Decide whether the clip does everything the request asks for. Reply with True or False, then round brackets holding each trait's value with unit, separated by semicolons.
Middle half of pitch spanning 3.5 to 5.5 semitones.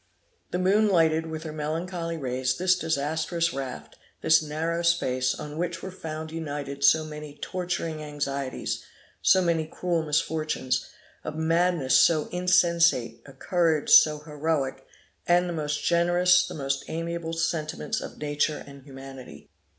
False (2.7 semitones)